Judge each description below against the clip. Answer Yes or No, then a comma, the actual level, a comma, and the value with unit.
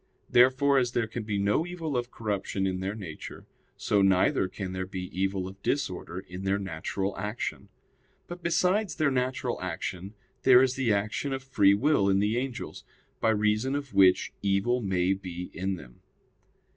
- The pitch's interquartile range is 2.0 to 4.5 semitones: No, average, 5.1 semitones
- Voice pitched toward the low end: Yes, low, 105 Hz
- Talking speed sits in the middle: Yes, average, 170 wpm